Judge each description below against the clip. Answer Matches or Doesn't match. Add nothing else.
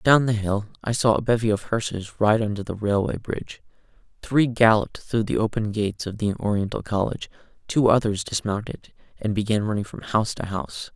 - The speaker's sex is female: Doesn't match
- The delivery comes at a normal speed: Matches